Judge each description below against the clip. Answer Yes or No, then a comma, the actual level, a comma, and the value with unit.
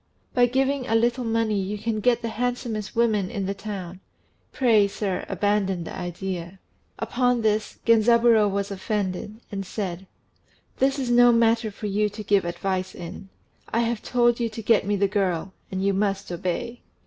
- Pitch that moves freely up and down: No, average, 3.2 semitones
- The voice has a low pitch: No, high, 210 Hz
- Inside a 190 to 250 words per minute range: No, average, 170 wpm